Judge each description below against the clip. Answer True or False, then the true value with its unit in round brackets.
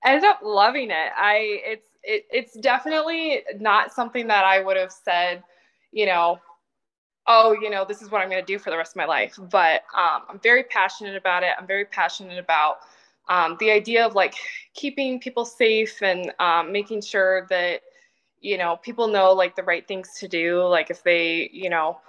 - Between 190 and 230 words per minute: True (195 wpm)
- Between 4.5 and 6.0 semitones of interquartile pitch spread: True (4.9 semitones)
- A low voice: False (195 Hz)